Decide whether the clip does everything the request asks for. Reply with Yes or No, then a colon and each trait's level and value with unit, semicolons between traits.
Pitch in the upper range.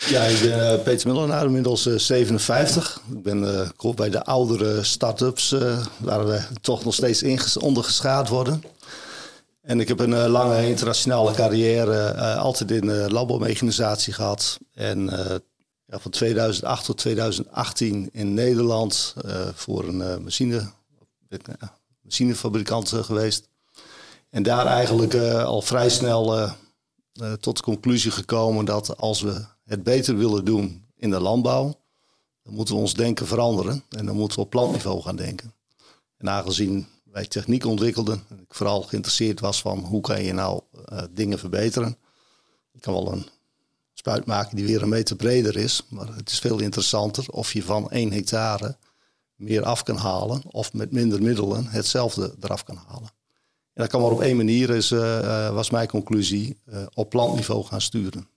No: low, 110 Hz